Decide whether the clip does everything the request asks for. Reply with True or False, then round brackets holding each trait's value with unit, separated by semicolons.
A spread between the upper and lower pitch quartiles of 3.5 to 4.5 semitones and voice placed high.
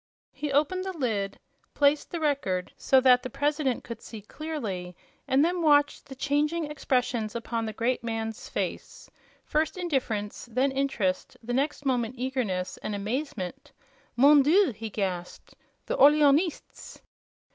False (5.0 semitones; 260 Hz)